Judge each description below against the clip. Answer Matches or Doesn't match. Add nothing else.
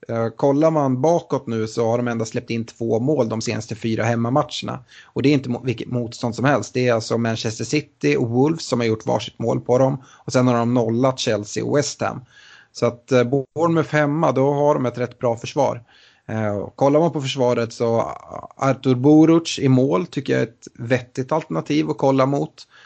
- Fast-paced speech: Matches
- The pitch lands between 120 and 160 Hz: Matches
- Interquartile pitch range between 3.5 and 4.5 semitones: Matches